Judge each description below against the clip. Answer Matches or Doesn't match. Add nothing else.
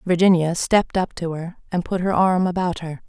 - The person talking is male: Doesn't match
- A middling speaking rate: Doesn't match